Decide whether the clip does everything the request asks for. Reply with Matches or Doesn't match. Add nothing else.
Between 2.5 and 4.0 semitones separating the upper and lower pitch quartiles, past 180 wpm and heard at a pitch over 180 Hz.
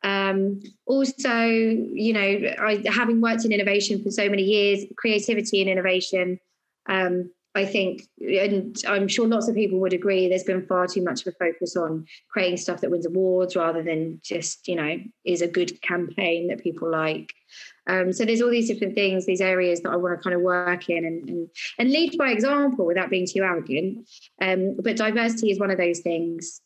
Matches